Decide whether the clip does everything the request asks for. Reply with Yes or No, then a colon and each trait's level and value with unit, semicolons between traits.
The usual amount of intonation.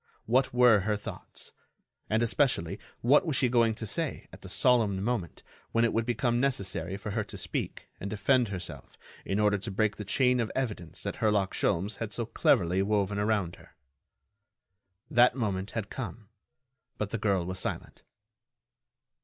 Yes: average, 3.4 semitones